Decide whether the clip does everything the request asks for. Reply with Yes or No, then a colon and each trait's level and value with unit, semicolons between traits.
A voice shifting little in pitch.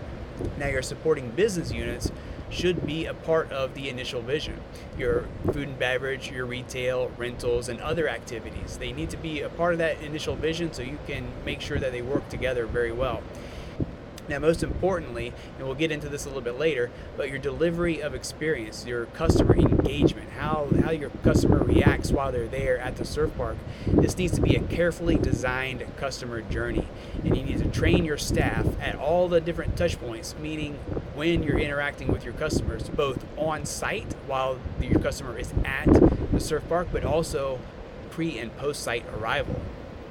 No: average, 4.6 semitones